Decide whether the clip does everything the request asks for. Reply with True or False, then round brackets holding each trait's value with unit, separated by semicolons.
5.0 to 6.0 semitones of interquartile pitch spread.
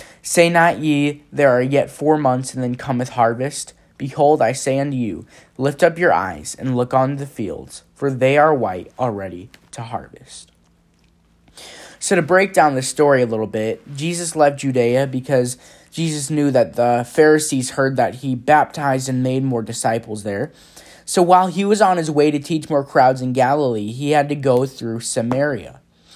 False (3.3 semitones)